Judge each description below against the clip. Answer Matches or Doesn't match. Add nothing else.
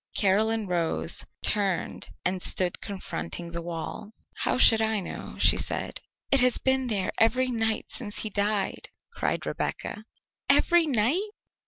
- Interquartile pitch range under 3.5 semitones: Doesn't match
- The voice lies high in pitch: Matches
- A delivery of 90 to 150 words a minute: Matches